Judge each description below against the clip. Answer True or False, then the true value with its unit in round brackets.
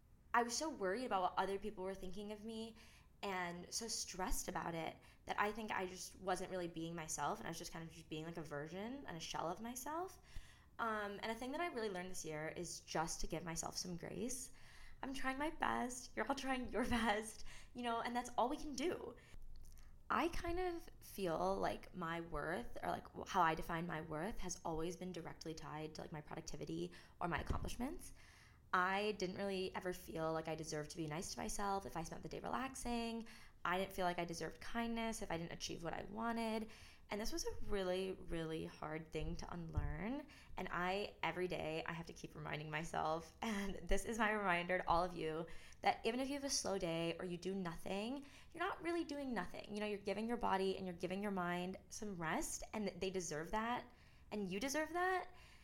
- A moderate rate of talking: False (220 wpm)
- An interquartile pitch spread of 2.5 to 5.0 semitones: False (5.4 semitones)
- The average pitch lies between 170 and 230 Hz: True (190 Hz)